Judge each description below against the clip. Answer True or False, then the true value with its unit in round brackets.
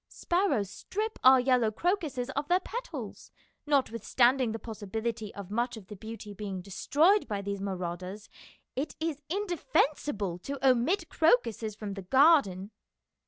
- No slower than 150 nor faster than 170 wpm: False (140 wpm)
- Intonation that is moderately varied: False (6.5 semitones)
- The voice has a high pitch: True (235 Hz)